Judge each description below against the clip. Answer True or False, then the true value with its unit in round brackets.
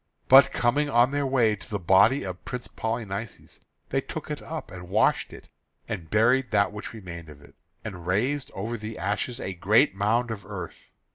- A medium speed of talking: True (190 wpm)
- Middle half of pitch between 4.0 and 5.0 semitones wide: True (4.3 semitones)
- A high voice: False (110 Hz)